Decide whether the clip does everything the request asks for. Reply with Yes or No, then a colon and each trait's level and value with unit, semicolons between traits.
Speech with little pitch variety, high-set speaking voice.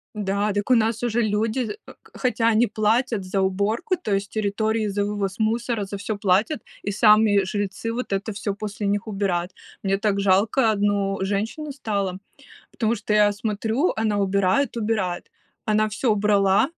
Yes: narrow, 2.1 semitones; high, 210 Hz